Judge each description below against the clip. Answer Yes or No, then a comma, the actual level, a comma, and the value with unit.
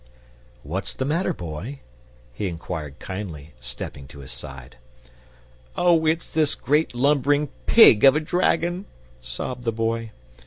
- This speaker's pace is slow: Yes, slow, 130 wpm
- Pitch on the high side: No, low, 115 Hz